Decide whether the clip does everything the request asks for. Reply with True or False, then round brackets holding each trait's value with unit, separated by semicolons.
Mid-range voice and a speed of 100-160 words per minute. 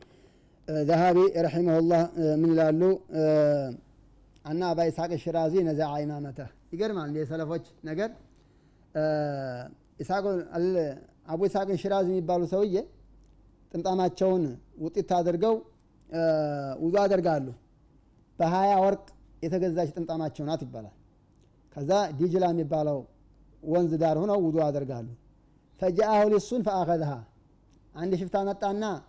False (165 Hz; 85 wpm)